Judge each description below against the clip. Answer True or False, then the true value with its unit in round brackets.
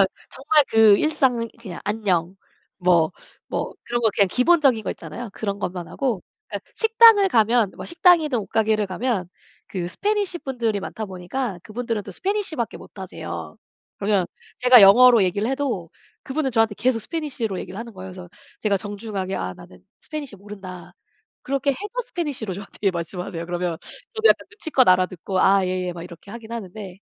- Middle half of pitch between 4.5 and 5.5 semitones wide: False (5.9 semitones)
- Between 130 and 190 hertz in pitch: False (215 Hz)